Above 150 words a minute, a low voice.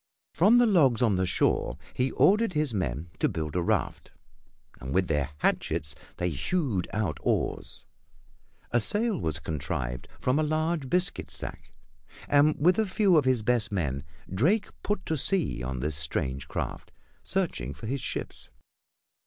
Yes: average, 160 wpm; low, 120 Hz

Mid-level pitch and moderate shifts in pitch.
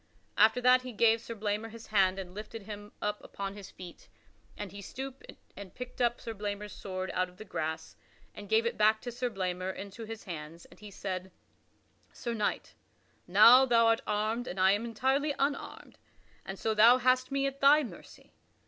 No: high, 215 Hz; average, 3.6 semitones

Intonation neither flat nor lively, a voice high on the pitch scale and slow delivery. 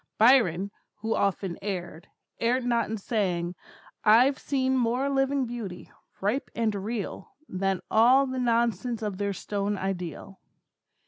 Yes: average, 4.1 semitones; high, 220 Hz; slow, 130 wpm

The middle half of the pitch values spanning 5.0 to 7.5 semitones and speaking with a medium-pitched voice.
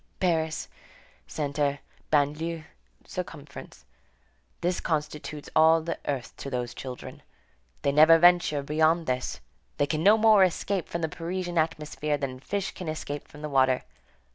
No: average, 2.9 semitones; medium, 155 Hz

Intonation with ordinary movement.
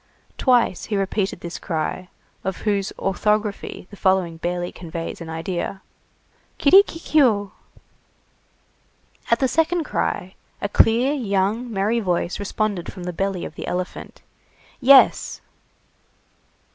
Yes: average, 4.4 semitones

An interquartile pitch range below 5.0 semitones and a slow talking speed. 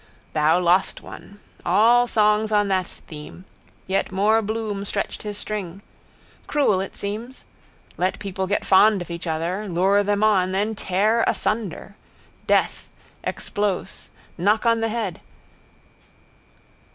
Yes: narrow, 2.5 semitones; slow, 130 wpm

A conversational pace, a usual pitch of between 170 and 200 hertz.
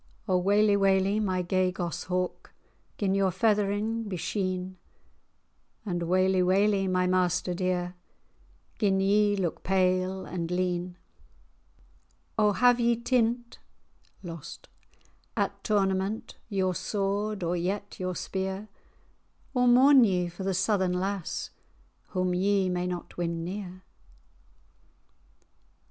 No: slow, 115 wpm; high, 190 Hz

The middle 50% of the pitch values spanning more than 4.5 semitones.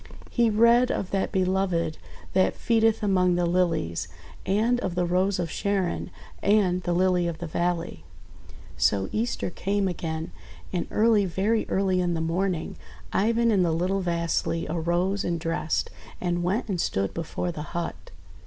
No: average, 2.8 semitones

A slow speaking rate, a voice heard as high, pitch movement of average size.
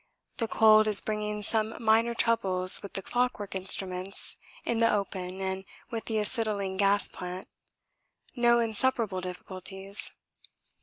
Yes: slow, 125 wpm; high, 210 Hz; average, 3.0 semitones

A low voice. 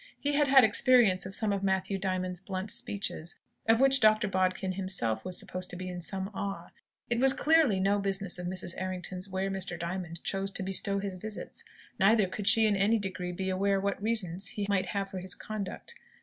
No: high, 195 Hz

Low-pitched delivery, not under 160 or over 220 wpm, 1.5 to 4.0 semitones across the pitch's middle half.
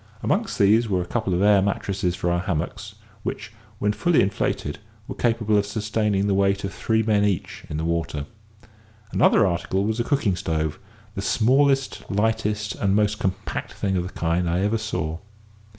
Yes: low, 100 Hz; average, 180 wpm; average, 3.1 semitones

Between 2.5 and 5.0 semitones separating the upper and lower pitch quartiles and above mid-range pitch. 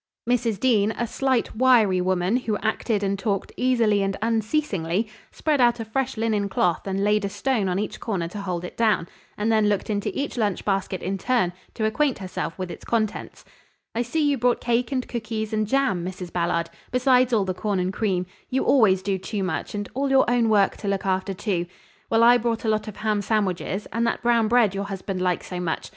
Yes: average, 3.6 semitones; high, 215 Hz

